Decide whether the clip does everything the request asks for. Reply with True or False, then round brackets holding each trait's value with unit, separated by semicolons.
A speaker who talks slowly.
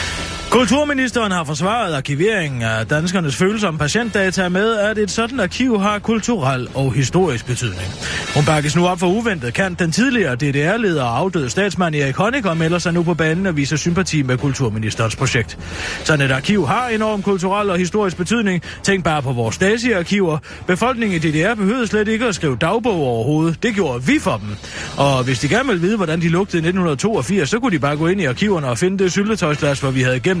False (200 wpm)